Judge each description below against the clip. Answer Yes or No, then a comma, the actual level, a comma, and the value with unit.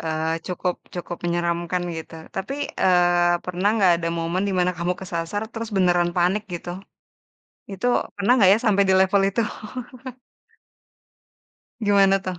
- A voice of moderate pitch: Yes, medium, 180 Hz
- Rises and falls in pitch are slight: Yes, narrow, 2.2 semitones